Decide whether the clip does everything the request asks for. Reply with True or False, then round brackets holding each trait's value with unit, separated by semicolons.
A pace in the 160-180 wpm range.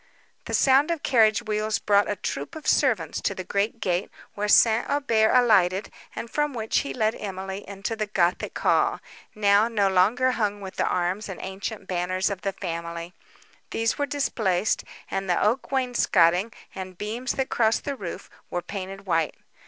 True (175 wpm)